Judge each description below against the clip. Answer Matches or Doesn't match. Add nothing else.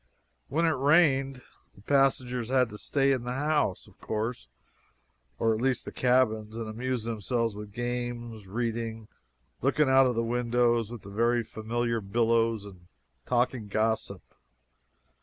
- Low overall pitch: Matches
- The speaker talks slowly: Doesn't match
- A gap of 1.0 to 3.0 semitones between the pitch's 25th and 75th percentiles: Matches